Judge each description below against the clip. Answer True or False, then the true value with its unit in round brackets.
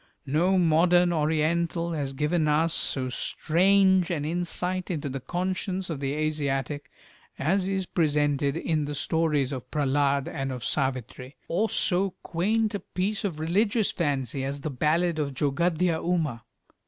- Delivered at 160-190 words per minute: False (145 wpm)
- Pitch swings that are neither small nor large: True (3.9 semitones)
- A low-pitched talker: False (160 Hz)